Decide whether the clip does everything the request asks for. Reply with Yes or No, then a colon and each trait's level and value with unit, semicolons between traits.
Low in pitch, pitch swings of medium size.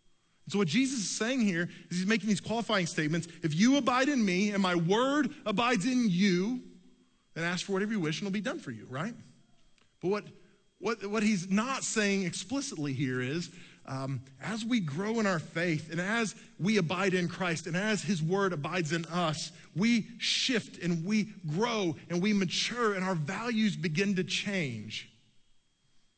No: high, 195 Hz; average, 4.2 semitones